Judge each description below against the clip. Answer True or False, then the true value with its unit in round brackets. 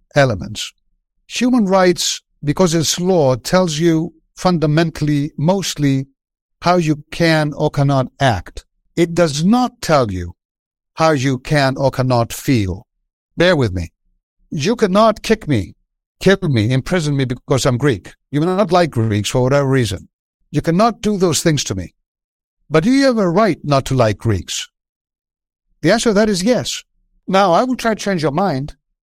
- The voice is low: False (150 Hz)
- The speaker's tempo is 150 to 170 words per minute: True (165 wpm)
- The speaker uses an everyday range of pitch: False (5.9 semitones)